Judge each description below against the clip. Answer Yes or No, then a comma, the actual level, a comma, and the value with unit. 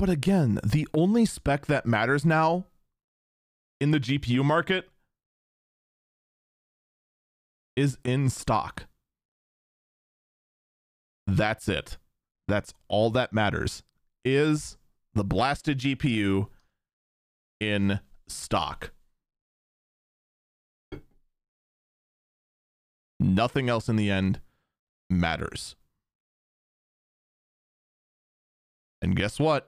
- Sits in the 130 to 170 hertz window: No, low, 120 Hz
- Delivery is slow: Yes, slow, 75 wpm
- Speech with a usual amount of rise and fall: No, wide, 7.2 semitones